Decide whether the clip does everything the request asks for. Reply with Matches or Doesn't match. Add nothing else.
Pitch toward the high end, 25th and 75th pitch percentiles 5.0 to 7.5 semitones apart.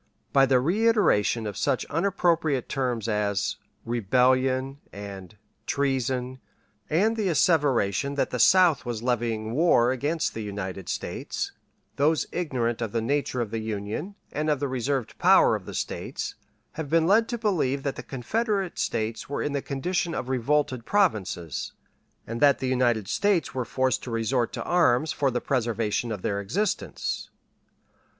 Doesn't match